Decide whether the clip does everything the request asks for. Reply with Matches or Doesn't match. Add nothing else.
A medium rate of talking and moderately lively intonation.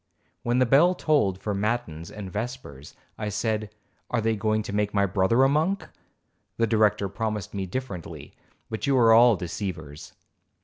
Matches